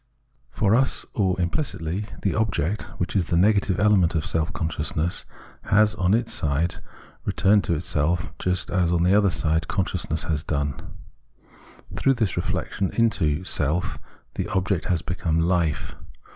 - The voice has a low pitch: Yes, very low, 90 Hz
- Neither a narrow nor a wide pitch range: Yes, average, 3.8 semitones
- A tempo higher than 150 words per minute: No, average, 145 wpm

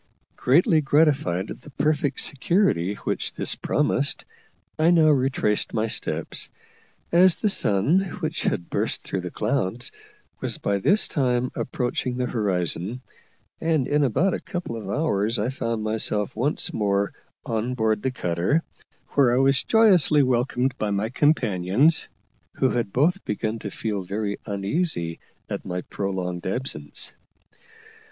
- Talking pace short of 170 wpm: Yes, average, 140 wpm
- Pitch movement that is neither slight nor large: No, wide, 6.5 semitones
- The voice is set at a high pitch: No, low, 120 Hz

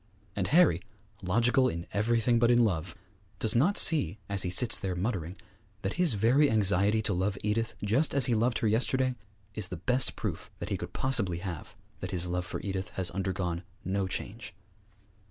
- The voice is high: No, low, 105 Hz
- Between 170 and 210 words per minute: Yes, average, 185 wpm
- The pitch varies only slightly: No, average, 4.4 semitones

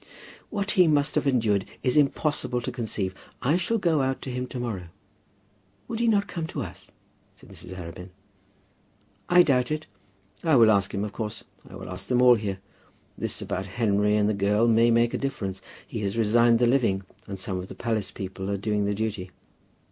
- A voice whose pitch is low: Yes, low, 115 Hz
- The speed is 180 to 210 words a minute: Yes, average, 200 wpm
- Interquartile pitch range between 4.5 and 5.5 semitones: Yes, average, 5.2 semitones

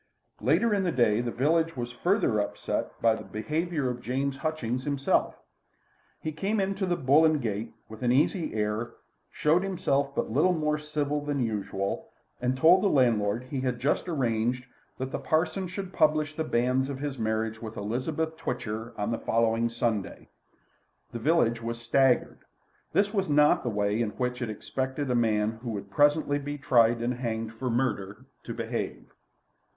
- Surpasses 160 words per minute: Yes, average, 175 wpm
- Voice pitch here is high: No, low, 130 Hz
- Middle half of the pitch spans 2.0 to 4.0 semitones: No, average, 4.9 semitones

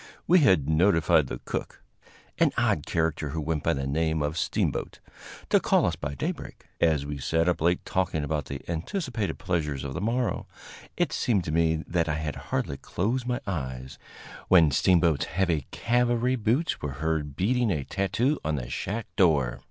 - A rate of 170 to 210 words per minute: Yes, average, 175 wpm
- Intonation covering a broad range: No, average, 5.0 semitones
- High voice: No, very low, 80 Hz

